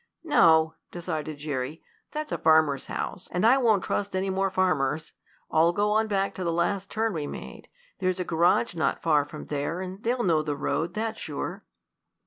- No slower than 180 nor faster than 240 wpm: Yes, average, 185 wpm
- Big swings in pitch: No, average, 4.1 semitones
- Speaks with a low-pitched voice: No, medium, 175 Hz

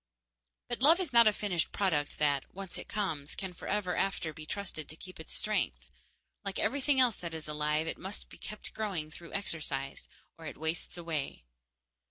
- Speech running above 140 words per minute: Yes, average, 185 wpm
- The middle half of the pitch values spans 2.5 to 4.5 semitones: No, average, 5.2 semitones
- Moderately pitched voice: Yes, medium, 175 Hz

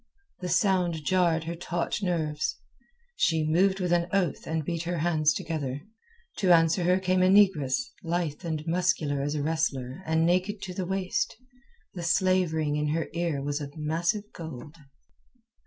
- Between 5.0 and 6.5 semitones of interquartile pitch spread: No, average, 2.9 semitones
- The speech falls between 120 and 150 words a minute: No, average, 165 wpm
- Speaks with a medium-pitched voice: Yes, medium, 170 Hz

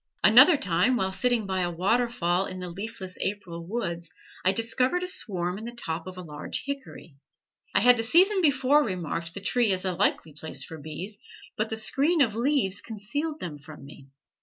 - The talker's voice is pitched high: Yes, high, 200 Hz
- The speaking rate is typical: Yes, average, 190 wpm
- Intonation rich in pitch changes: Yes, wide, 6.0 semitones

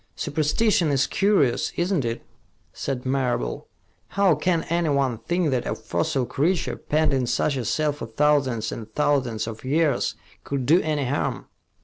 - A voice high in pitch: No, medium, 145 Hz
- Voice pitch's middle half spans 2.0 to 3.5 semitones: No, average, 4.0 semitones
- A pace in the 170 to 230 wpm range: No, average, 150 wpm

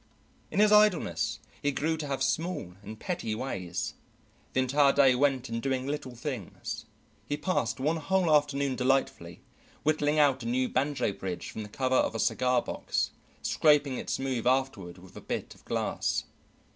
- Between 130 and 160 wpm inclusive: No, average, 170 wpm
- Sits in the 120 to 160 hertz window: Yes, low, 135 Hz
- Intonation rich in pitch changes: No, average, 3.4 semitones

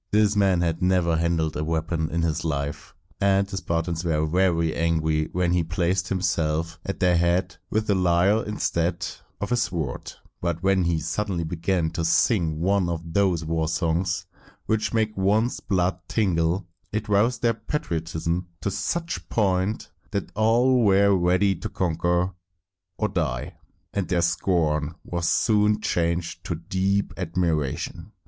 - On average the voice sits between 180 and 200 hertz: No, very low, 90 Hz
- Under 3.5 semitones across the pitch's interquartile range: Yes, average, 3.1 semitones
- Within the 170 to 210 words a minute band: No, average, 155 wpm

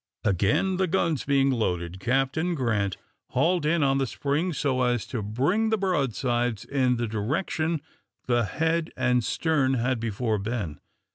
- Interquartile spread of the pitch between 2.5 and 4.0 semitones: No, wide, 5.5 semitones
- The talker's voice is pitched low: Yes, low, 130 Hz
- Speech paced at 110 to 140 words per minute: No, average, 150 wpm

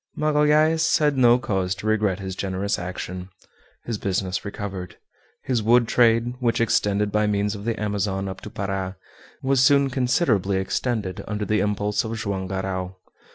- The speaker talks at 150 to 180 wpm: Yes, average, 155 wpm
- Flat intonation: No, average, 3.9 semitones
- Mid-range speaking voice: No, low, 105 Hz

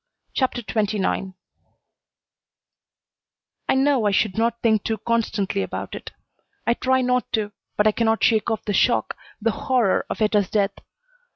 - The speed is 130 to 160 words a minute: Yes, average, 150 wpm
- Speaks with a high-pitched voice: Yes, high, 220 Hz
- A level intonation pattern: Yes, narrow, 2.3 semitones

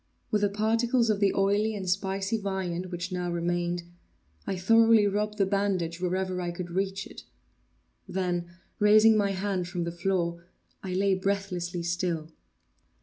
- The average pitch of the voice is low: No, high, 190 Hz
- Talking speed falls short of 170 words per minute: Yes, average, 150 wpm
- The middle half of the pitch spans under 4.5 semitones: Yes, narrow, 2.5 semitones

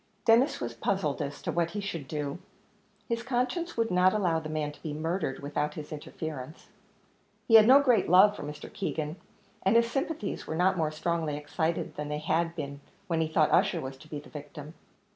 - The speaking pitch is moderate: Yes, medium, 160 Hz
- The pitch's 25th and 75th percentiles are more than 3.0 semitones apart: Yes, average, 5.1 semitones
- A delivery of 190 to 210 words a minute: Yes, average, 200 wpm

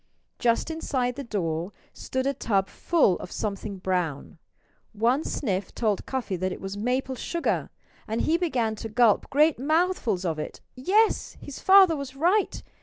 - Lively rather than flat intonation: Yes, wide, 7.1 semitones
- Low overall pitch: No, high, 245 Hz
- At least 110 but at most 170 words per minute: Yes, average, 160 wpm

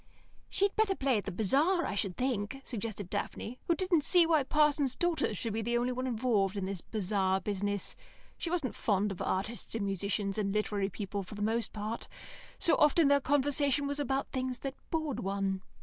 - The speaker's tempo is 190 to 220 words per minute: Yes, average, 195 wpm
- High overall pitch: Yes, high, 230 Hz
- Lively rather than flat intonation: Yes, wide, 6.0 semitones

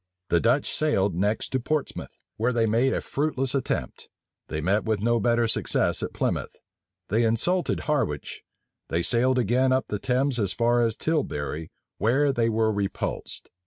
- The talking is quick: No, average, 160 wpm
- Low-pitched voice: Yes, low, 115 Hz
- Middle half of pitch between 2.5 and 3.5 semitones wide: No, average, 4.1 semitones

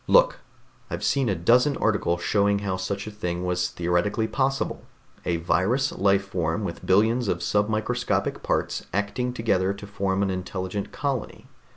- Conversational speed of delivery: Yes, average, 155 wpm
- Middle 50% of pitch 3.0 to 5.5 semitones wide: Yes, average, 3.4 semitones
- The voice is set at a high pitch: No, low, 100 Hz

